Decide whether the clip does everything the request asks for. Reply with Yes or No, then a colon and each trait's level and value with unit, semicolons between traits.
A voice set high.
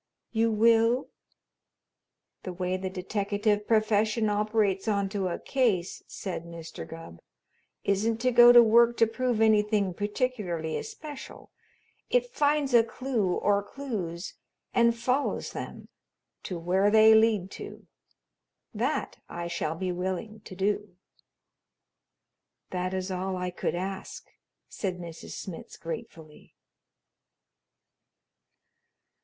Yes: high, 205 Hz